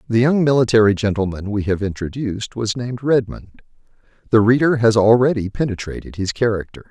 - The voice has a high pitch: No, low, 115 Hz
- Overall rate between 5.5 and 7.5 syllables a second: Yes, 5.8 syllables/s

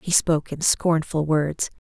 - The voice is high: No, medium, 160 Hz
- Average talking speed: Yes, average, 160 wpm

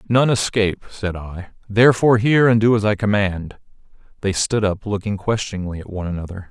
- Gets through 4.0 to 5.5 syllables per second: No, 5.9 syllables/s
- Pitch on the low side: Yes, low, 105 Hz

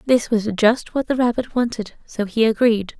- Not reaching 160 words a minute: No, average, 200 wpm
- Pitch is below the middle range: No, high, 230 Hz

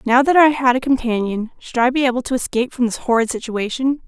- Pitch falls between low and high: No, very high, 250 Hz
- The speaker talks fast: Yes, fast, 235 wpm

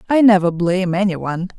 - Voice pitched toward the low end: No, high, 190 Hz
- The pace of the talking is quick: No, average, 150 wpm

